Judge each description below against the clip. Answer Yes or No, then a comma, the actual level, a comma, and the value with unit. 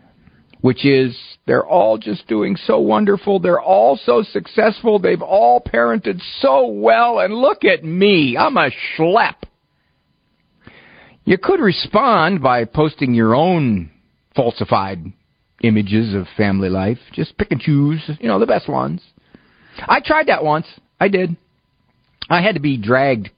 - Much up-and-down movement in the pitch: Yes, wide, 8.7 semitones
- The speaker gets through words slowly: No, average, 145 wpm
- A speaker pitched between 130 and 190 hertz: Yes, low, 135 Hz